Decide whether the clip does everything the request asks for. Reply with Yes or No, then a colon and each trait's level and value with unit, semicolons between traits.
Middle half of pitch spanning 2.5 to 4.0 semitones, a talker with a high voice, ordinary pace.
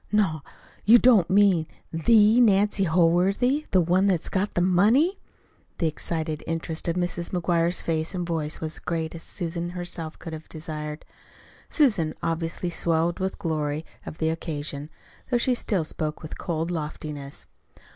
No: average, 3.1 semitones; medium, 170 Hz; average, 160 wpm